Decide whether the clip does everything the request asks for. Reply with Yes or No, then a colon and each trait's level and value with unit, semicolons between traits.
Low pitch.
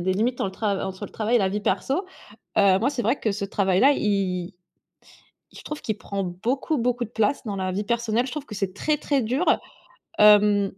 No: high, 210 Hz